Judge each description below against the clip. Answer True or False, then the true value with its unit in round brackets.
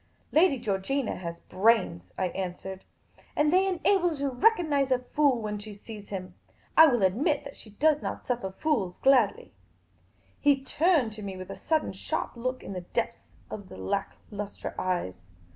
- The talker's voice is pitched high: True (230 Hz)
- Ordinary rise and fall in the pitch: False (7.0 semitones)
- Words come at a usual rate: True (180 wpm)